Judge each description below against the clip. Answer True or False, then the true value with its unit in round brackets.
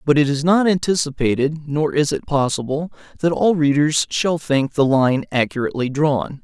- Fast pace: False (170 wpm)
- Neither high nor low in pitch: True (150 Hz)